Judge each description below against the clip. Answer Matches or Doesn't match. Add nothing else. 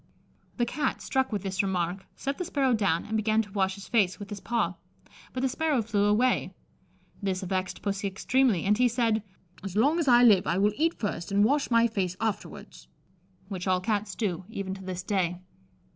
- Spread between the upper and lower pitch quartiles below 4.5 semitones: Matches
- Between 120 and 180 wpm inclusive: Doesn't match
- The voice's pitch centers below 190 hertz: Doesn't match